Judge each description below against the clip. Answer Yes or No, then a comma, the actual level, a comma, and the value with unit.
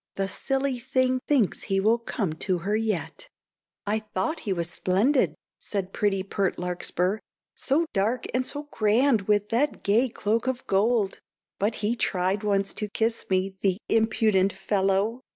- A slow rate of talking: No, average, 155 wpm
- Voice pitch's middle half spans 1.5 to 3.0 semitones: No, average, 3.4 semitones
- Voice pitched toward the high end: Yes, high, 210 Hz